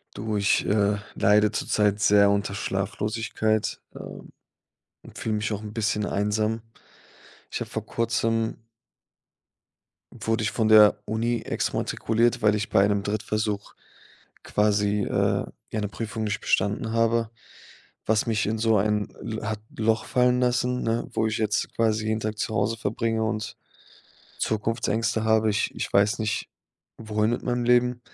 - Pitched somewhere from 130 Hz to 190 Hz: No, low, 110 Hz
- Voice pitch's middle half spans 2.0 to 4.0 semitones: No, narrow, 1.4 semitones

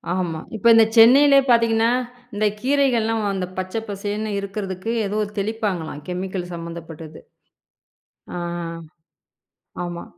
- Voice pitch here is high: Yes, high, 205 Hz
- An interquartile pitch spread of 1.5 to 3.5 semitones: No, average, 3.9 semitones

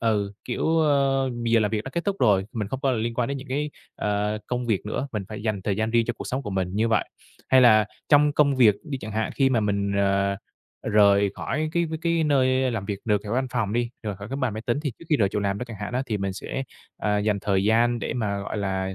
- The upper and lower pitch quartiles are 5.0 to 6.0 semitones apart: No, average, 4.4 semitones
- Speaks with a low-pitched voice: Yes, low, 110 Hz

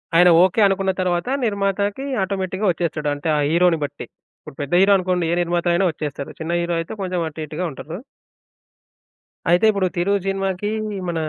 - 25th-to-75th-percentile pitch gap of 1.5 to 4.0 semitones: Yes, average, 2.7 semitones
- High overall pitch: No, medium, 180 Hz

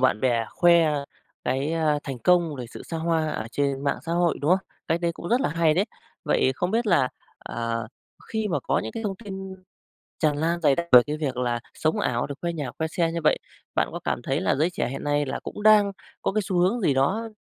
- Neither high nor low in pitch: Yes, medium, 160 Hz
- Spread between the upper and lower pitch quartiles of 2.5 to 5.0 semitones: Yes, average, 4.6 semitones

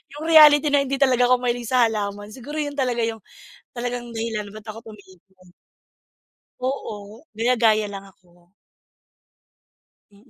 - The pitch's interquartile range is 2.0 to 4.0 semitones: Yes, average, 3.5 semitones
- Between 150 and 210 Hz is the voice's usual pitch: No, high, 230 Hz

